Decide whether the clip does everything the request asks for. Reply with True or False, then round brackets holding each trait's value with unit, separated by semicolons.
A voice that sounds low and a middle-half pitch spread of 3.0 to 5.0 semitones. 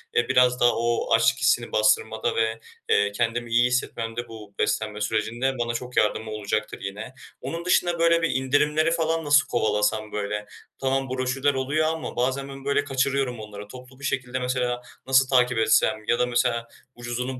True (125 Hz; 3.4 semitones)